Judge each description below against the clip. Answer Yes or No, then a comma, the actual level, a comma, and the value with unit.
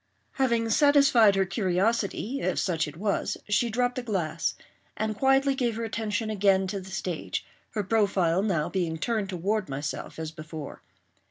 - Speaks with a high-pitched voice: Yes, high, 205 Hz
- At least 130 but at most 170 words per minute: Yes, average, 150 wpm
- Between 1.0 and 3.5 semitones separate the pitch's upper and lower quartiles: No, average, 4.1 semitones